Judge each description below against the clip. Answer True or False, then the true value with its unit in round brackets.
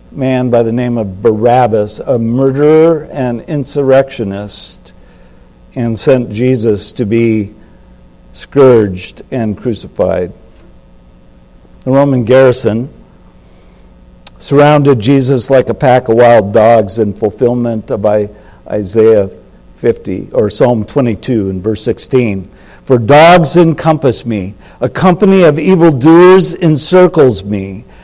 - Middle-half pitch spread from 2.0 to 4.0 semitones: False (4.7 semitones)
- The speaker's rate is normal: False (105 wpm)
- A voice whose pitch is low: True (120 Hz)